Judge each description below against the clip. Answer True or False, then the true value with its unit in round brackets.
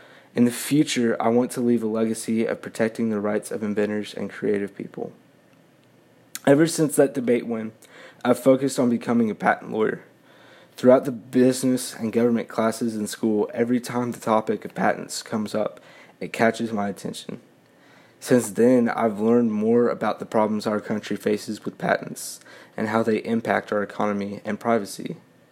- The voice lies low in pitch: True (115 Hz)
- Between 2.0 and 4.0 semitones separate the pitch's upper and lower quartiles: True (2.5 semitones)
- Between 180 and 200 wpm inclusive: False (165 wpm)